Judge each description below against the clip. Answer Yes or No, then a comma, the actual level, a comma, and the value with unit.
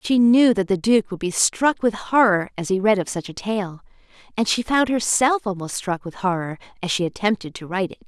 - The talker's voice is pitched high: Yes, high, 205 Hz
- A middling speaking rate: No, fast, 230 wpm